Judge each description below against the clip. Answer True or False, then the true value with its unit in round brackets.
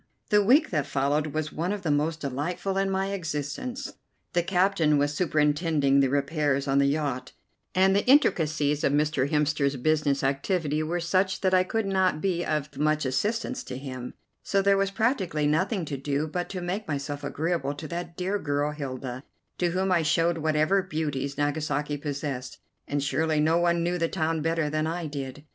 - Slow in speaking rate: False (185 wpm)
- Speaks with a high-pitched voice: False (155 Hz)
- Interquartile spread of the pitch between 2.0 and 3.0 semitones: False (3.9 semitones)